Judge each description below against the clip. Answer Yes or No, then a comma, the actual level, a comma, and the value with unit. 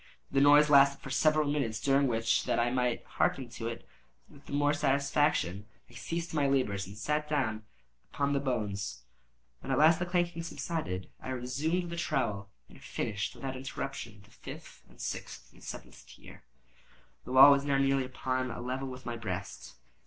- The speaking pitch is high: No, low, 135 Hz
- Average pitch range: Yes, average, 3.8 semitones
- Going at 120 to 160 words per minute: No, average, 180 wpm